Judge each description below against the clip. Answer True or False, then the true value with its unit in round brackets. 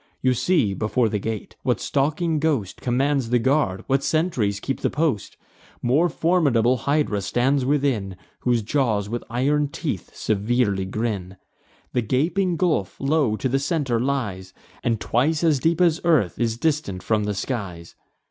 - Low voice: True (125 Hz)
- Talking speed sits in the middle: True (155 wpm)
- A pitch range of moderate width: False (5.7 semitones)